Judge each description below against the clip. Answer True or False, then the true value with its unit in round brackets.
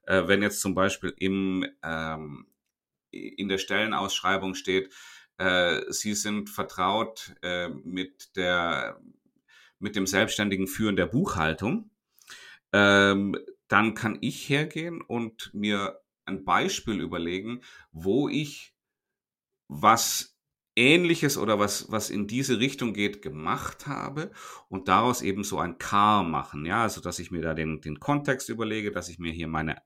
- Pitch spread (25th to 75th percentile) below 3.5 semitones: False (4.0 semitones)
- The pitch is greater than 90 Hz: True (100 Hz)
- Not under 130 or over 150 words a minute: True (140 wpm)